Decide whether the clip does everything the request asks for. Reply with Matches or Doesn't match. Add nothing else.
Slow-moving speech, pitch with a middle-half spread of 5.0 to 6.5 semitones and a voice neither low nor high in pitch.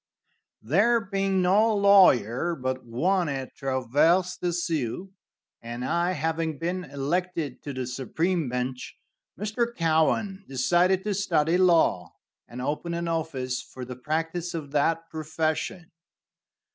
Matches